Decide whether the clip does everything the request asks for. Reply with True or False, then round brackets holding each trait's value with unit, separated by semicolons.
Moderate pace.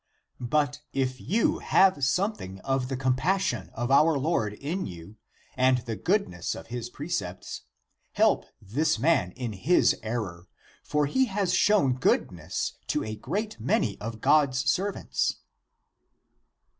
False (130 wpm)